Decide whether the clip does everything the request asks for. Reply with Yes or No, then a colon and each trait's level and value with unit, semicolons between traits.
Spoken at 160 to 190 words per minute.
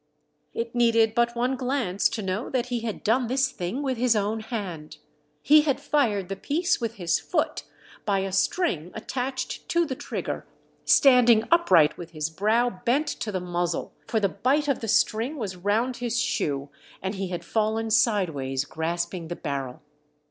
Yes: average, 175 wpm